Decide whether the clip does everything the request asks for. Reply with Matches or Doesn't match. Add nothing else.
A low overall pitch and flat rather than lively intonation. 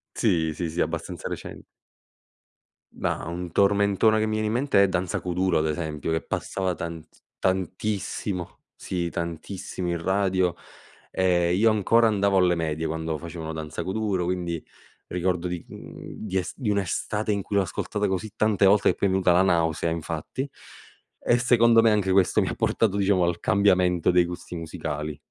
Doesn't match